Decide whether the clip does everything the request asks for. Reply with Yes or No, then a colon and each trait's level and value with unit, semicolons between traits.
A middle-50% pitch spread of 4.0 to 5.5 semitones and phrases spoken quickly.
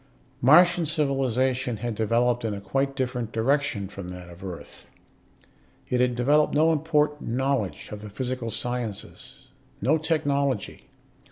No: average, 4.3 semitones; slow, 135 wpm